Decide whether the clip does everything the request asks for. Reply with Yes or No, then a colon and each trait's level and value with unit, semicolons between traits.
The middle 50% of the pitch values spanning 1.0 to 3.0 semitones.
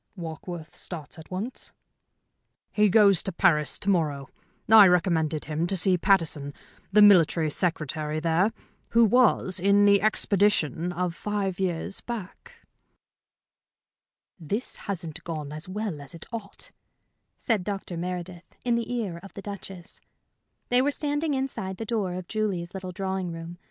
No: average, 3.7 semitones